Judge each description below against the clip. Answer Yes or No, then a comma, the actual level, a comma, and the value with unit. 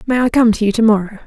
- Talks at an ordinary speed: No, fast, 330 wpm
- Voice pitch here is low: No, high, 225 Hz